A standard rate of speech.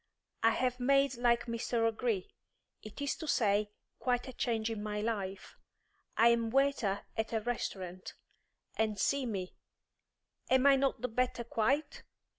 Yes: average, 150 wpm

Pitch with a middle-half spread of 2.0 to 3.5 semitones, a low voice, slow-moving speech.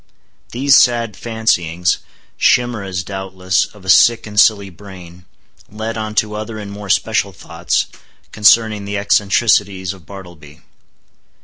Yes: average, 2.8 semitones; low, 100 Hz; slow, 115 wpm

